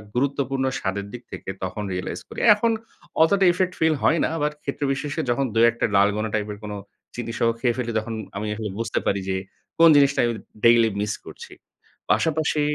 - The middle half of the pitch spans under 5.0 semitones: No, wide, 5.5 semitones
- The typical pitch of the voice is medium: No, low, 120 Hz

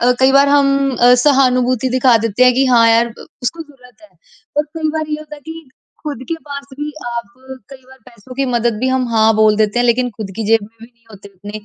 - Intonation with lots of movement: No, average, 3.3 semitones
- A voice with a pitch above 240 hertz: Yes, very high, 250 Hz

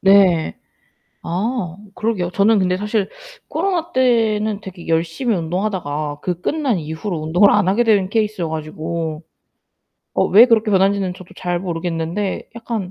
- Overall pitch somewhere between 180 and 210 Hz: Yes, high, 190 Hz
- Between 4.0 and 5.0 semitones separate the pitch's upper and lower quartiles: Yes, average, 4.3 semitones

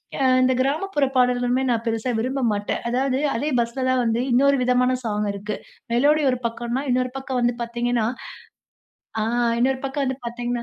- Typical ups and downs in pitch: No, narrow, 1.9 semitones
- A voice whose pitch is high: Yes, very high, 250 Hz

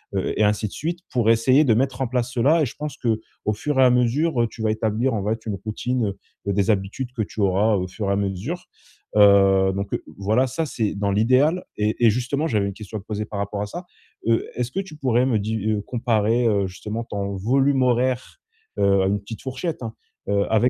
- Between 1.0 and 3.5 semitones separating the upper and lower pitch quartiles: No, average, 4.0 semitones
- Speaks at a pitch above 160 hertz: No, low, 110 Hz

